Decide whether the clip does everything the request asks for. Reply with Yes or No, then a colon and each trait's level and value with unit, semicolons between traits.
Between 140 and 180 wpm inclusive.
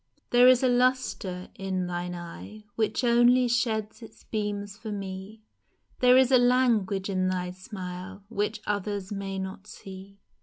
Yes: average, 150 wpm